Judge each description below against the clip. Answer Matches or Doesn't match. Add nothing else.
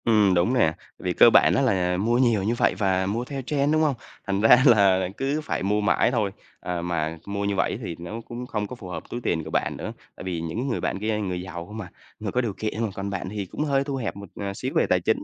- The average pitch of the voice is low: Matches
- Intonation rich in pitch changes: Doesn't match